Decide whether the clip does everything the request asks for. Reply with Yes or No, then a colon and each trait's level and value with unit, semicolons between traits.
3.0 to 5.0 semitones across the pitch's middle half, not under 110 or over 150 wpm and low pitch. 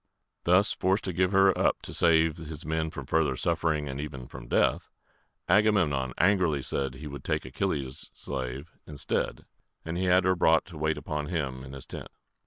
No: average, 4.4 semitones; average, 185 wpm; very low, 80 Hz